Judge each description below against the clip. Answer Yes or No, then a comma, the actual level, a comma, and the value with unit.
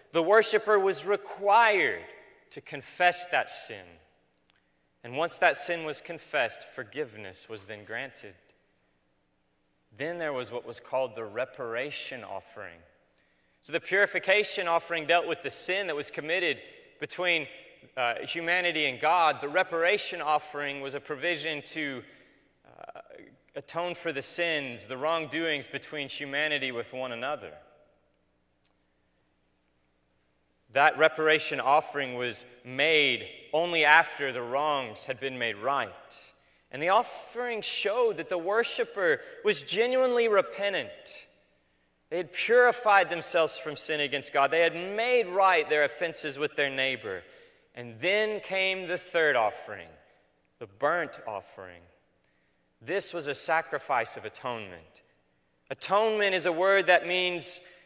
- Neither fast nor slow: No, slow, 130 wpm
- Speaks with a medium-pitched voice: Yes, medium, 155 Hz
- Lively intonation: Yes, wide, 6.4 semitones